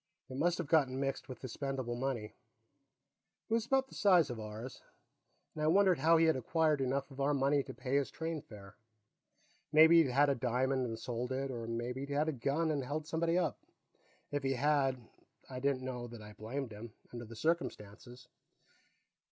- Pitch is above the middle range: No, low, 135 Hz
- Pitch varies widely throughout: No, average, 4.0 semitones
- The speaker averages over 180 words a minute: Yes, average, 195 wpm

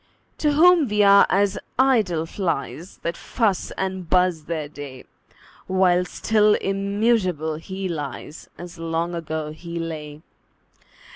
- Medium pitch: Yes, medium, 180 Hz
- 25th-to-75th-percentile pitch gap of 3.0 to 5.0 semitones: Yes, average, 3.8 semitones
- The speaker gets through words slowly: Yes, slow, 125 wpm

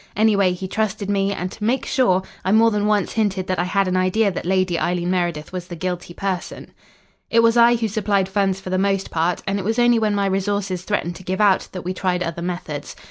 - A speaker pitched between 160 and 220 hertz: Yes, high, 190 Hz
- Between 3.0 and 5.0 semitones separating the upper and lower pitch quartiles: No, narrow, 2.4 semitones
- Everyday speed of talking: No, fast, 240 wpm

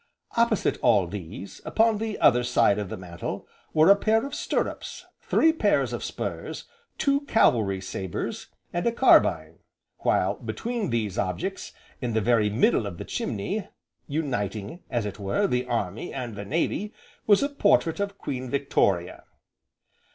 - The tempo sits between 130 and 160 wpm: Yes, average, 150 wpm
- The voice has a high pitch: No, low, 130 Hz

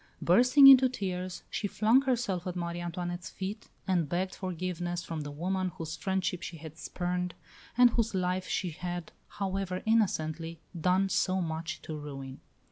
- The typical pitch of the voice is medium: Yes, medium, 180 Hz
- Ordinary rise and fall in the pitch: No, narrow, 2.3 semitones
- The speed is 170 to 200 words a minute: No, average, 155 wpm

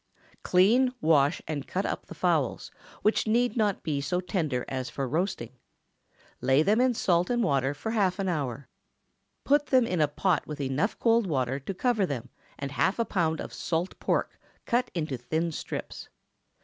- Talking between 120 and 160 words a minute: No, average, 185 wpm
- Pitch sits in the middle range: Yes, medium, 170 Hz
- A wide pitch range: Yes, wide, 7.1 semitones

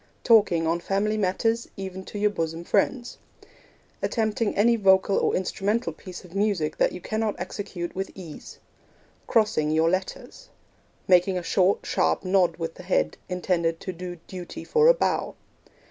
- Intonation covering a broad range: No, average, 3.3 semitones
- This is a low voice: No, high, 190 Hz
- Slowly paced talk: No, average, 155 wpm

